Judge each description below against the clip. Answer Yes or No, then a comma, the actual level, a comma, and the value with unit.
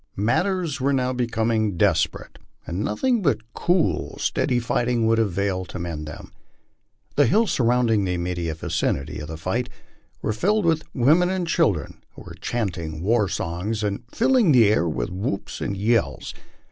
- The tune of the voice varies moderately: No, wide, 6.6 semitones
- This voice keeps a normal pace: Yes, average, 160 wpm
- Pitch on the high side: No, low, 110 Hz